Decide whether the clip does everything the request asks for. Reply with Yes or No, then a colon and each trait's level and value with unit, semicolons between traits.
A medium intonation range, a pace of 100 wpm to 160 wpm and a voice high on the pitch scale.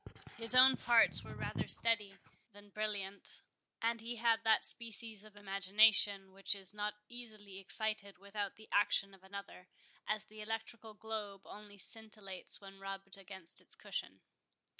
No: narrow, 2.1 semitones; average, 145 wpm; high, 205 Hz